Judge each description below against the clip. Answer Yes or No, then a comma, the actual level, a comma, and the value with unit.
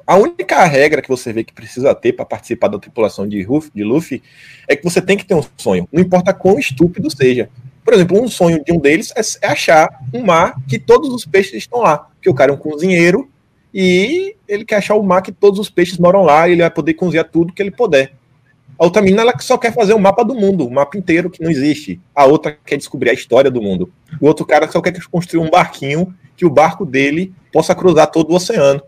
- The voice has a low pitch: No, medium, 170 Hz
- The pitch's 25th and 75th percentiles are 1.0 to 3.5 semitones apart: No, average, 5.1 semitones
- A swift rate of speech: Yes, fast, 245 wpm